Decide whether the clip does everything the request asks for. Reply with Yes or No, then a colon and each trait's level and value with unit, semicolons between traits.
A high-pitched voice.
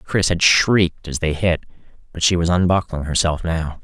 No: very low, 85 Hz